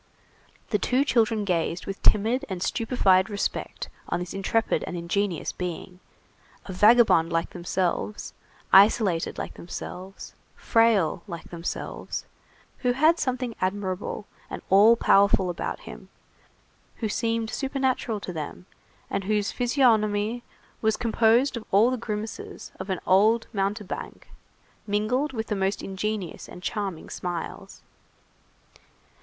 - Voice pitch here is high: Yes, high, 205 Hz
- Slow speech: Yes, slow, 125 wpm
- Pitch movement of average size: Yes, average, 3.7 semitones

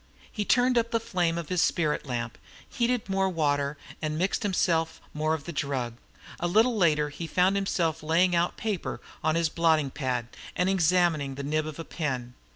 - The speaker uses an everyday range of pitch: Yes, average, 3.8 semitones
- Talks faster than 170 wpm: Yes, average, 185 wpm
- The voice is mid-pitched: Yes, medium, 165 Hz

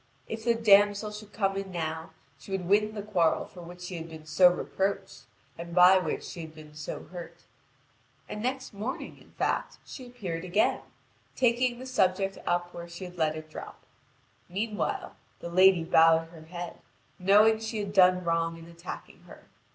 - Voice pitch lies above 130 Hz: Yes, medium, 185 Hz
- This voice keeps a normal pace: Yes, average, 180 wpm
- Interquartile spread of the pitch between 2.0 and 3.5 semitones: No, average, 3.9 semitones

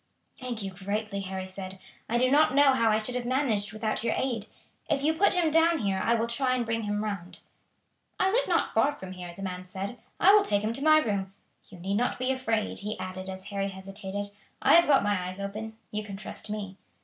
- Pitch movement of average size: Yes, average, 4.6 semitones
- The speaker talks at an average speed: No, fast, 230 wpm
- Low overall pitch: No, high, 215 Hz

